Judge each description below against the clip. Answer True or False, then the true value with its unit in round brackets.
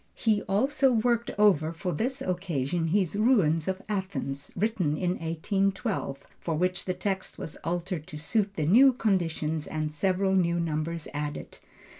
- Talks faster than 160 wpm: False (150 wpm)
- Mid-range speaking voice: True (180 Hz)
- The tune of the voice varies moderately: True (4.4 semitones)